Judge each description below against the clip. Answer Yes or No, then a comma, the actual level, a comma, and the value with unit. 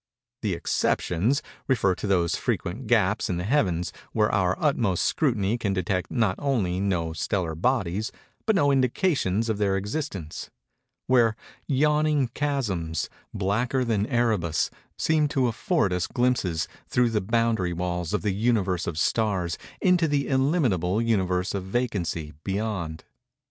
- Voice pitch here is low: Yes, low, 105 Hz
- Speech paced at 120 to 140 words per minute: Yes, slow, 135 wpm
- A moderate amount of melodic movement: No, wide, 5.8 semitones